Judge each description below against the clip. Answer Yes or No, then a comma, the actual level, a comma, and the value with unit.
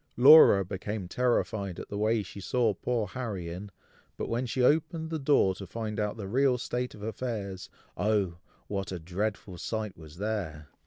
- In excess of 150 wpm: Yes, average, 175 wpm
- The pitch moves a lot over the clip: No, average, 4.2 semitones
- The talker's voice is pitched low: Yes, low, 105 Hz